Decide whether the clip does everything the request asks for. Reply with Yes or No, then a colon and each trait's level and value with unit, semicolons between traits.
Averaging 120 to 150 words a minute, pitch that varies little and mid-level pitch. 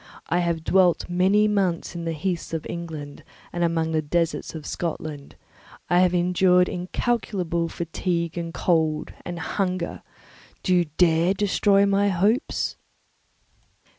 Yes: slow, 135 wpm; narrow, 2.1 semitones; medium, 175 Hz